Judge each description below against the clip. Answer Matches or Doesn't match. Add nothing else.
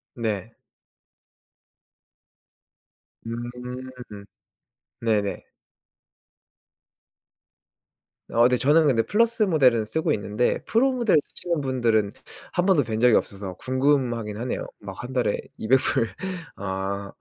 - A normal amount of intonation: Matches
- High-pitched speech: Doesn't match